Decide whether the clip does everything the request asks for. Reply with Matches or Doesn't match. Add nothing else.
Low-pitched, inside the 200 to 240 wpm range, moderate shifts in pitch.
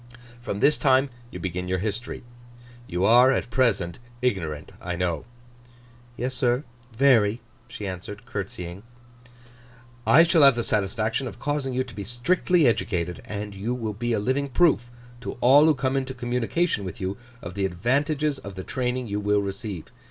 Doesn't match